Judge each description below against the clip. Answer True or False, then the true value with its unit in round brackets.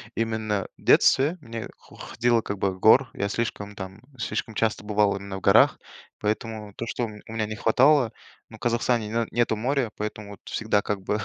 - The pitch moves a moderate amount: False (2.1 semitones)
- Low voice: True (110 Hz)